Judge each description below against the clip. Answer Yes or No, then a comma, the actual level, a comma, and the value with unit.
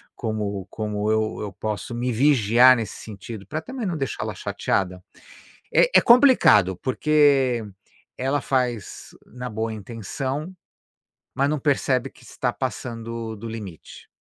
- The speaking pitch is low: Yes, low, 115 Hz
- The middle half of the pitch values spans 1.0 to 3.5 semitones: No, average, 4.1 semitones